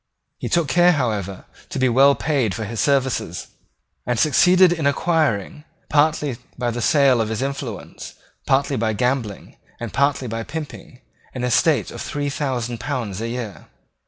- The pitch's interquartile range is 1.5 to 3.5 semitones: No, average, 4.1 semitones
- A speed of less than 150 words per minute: No, average, 160 wpm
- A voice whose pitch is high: No, low, 130 Hz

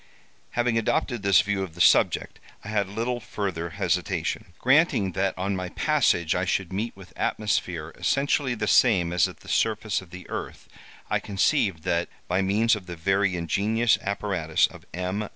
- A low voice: Yes, low, 100 Hz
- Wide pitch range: No, average, 3.5 semitones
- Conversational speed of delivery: Yes, average, 170 wpm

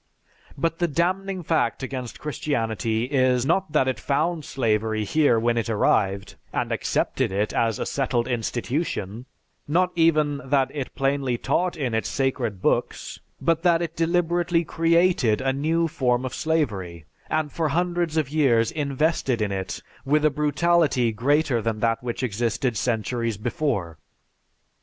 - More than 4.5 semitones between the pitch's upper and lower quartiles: Yes, wide, 5.6 semitones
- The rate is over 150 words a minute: No, average, 145 wpm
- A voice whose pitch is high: No, low, 135 Hz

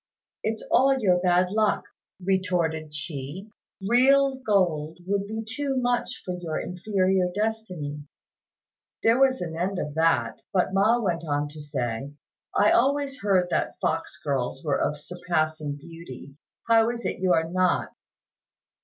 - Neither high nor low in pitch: Yes, medium, 180 Hz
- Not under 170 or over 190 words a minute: No, average, 145 wpm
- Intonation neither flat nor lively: No, wide, 5.8 semitones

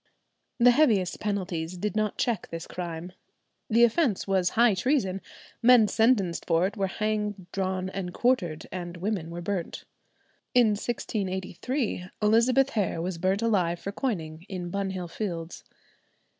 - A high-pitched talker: Yes, high, 195 Hz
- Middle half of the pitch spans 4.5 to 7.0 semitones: No, average, 3.9 semitones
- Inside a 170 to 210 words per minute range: No, average, 140 wpm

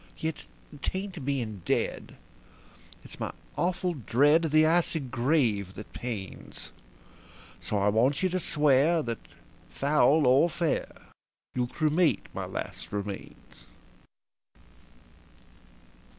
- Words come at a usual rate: No, slow, 110 wpm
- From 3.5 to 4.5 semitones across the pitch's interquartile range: No, wide, 5.5 semitones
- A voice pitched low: No, medium, 145 Hz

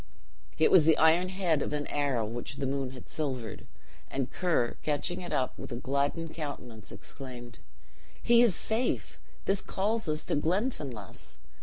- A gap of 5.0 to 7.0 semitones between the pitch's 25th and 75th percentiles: Yes, average, 5.3 semitones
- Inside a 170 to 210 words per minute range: No, average, 160 wpm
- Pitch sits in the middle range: Yes, medium, 145 Hz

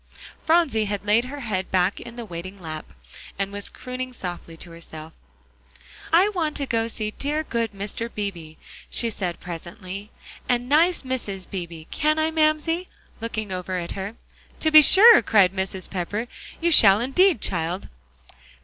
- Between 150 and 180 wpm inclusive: Yes, average, 160 wpm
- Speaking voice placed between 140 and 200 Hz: No, high, 215 Hz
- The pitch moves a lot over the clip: Yes, wide, 7.3 semitones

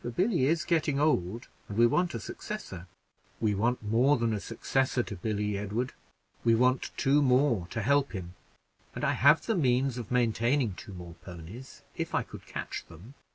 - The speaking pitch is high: No, low, 120 Hz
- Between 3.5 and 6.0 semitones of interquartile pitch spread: Yes, average, 4.8 semitones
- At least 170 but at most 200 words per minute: Yes, average, 185 wpm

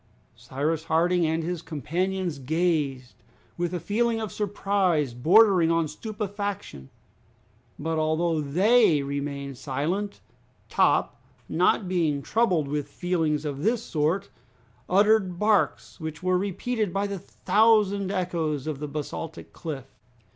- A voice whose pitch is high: No, medium, 170 Hz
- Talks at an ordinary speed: No, slow, 120 wpm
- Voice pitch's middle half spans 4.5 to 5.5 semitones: Yes, average, 4.9 semitones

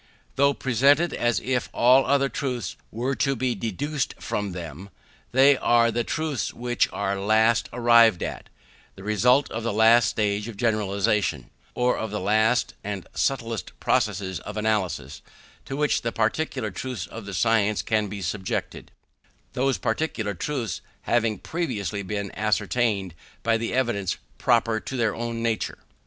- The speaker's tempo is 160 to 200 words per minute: No, average, 150 wpm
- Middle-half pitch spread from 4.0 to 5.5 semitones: No, average, 3.3 semitones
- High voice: No, low, 115 Hz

